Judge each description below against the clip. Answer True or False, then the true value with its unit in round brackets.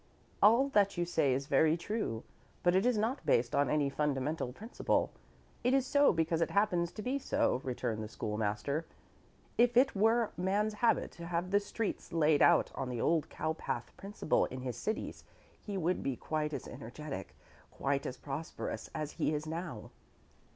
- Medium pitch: True (165 Hz)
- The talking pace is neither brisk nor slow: True (180 wpm)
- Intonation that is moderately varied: False (7.0 semitones)